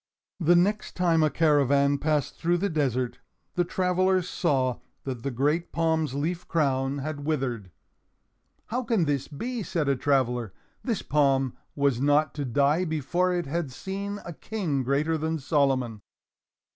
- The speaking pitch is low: No, medium, 150 Hz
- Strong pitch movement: No, average, 4.2 semitones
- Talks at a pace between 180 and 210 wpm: No, average, 150 wpm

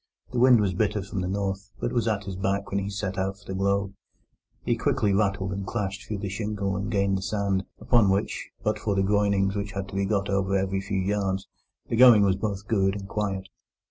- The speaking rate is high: Yes, fast, 230 wpm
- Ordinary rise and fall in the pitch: No, narrow, 1.2 semitones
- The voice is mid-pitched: No, low, 100 Hz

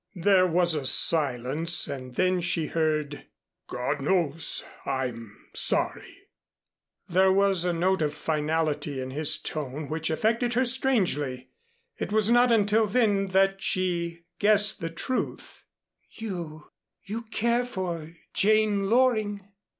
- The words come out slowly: Yes, slow, 125 wpm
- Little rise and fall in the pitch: No, average, 5.3 semitones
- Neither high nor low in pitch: Yes, medium, 180 Hz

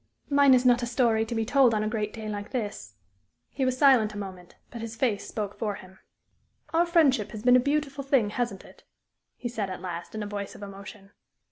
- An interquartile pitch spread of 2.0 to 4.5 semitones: Yes, average, 3.8 semitones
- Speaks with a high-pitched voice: Yes, high, 220 Hz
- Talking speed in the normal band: No, fast, 225 wpm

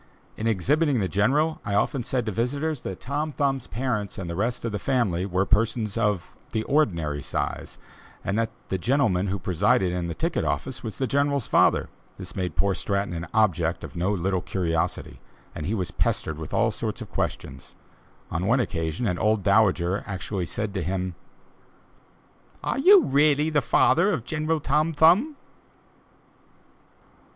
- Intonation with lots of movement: Yes, wide, 7.2 semitones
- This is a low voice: Yes, low, 110 Hz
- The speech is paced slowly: No, average, 165 wpm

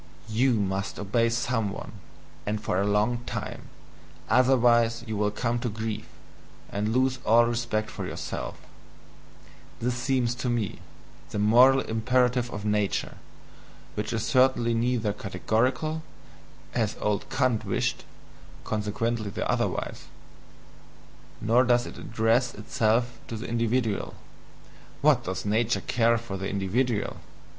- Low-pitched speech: Yes, low, 115 Hz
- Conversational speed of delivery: No, slow, 130 wpm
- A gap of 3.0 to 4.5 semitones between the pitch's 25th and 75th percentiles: No, narrow, 2.6 semitones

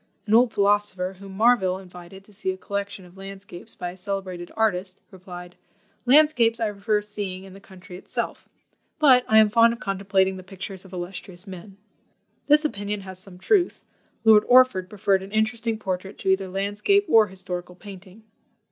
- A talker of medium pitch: No, high, 195 Hz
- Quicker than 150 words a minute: Yes, average, 170 wpm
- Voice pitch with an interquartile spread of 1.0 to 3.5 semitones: Yes, average, 2.7 semitones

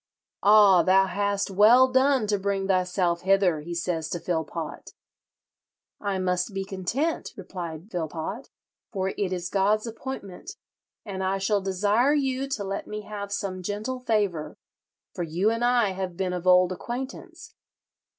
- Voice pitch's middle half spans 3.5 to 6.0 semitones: No, average, 3.1 semitones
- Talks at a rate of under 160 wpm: Yes, average, 150 wpm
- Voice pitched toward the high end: Yes, high, 195 Hz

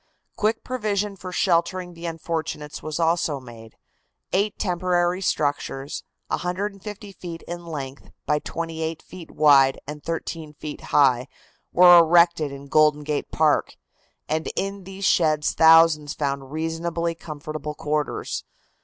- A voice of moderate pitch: Yes, medium, 165 Hz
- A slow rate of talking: Yes, slow, 125 wpm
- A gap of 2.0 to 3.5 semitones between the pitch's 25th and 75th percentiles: Yes, average, 2.9 semitones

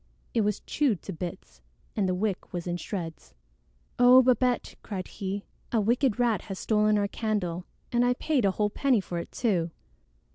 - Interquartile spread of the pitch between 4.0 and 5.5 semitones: Yes, average, 4.6 semitones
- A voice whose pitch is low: No, high, 210 Hz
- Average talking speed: Yes, average, 180 wpm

